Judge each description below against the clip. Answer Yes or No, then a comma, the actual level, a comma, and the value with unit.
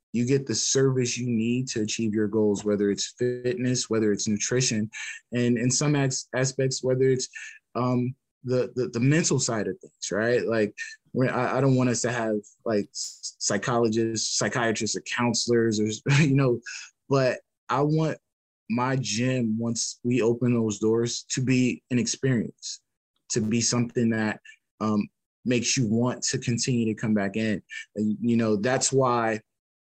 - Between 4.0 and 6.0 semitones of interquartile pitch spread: No, narrow, 2.5 semitones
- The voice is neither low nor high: No, low, 120 Hz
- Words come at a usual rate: Yes, average, 160 wpm